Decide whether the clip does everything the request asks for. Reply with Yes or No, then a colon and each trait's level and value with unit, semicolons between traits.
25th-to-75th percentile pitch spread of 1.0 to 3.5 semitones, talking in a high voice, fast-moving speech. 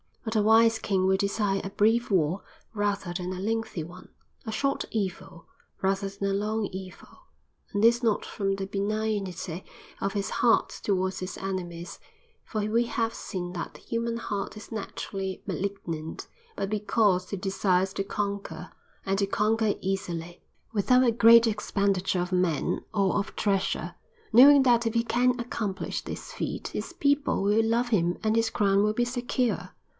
No: average, 2.9 semitones; high, 200 Hz; average, 165 wpm